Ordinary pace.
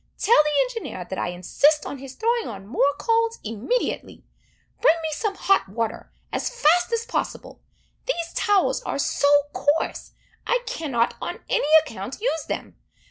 Yes: average, 155 wpm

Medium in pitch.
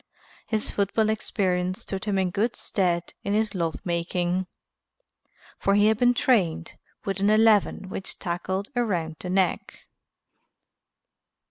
No: high, 195 Hz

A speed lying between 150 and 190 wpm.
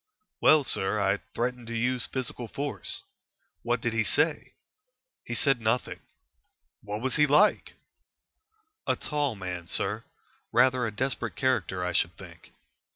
No: average, 140 wpm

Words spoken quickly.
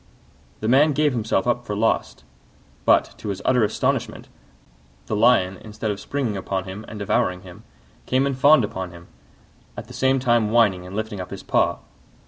No: average, 180 wpm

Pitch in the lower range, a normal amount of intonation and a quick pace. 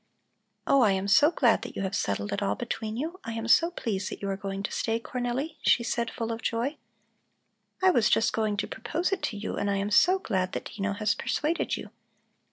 No: high, 225 Hz; average, 4.5 semitones; fast, 230 wpm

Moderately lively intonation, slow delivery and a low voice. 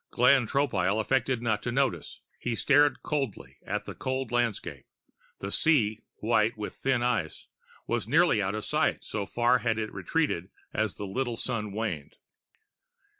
No: average, 4.0 semitones; average, 160 wpm; low, 115 Hz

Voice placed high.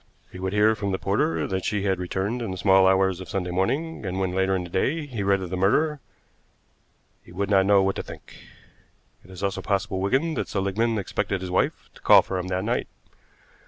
No: very low, 95 Hz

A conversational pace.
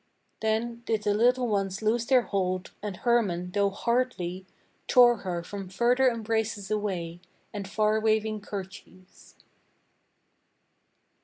No: slow, 115 wpm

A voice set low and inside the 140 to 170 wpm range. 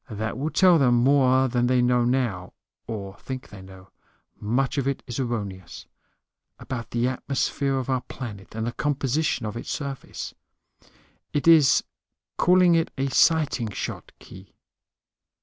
Yes: low, 125 Hz; average, 150 wpm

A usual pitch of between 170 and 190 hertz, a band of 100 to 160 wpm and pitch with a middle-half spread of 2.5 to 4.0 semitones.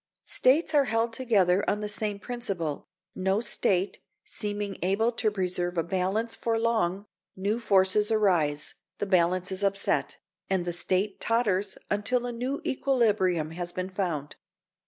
No: high, 200 Hz; average, 145 wpm; average, 3.7 semitones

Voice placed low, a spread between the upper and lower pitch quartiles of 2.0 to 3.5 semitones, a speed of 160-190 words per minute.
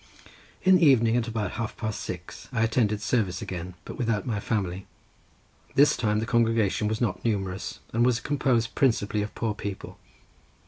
Yes: low, 110 Hz; narrow, 2.4 semitones; average, 170 wpm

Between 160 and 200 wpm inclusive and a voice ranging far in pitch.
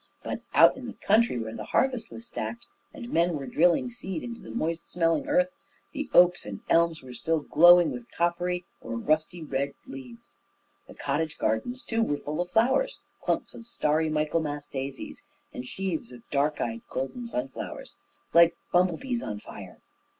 Yes: average, 170 wpm; wide, 8.2 semitones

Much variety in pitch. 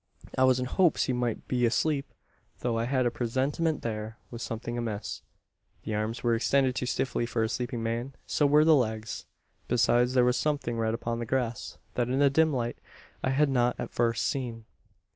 No: narrow, 2.4 semitones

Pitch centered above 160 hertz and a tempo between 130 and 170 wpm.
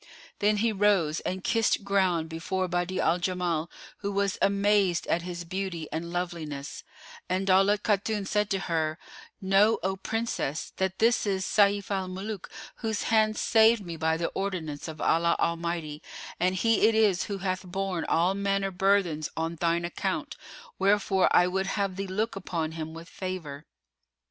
Yes: medium, 185 Hz; average, 165 wpm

